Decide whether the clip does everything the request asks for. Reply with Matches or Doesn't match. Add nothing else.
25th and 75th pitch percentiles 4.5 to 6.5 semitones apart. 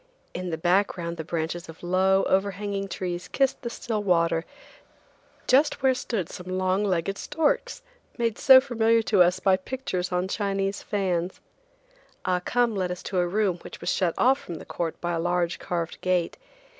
Doesn't match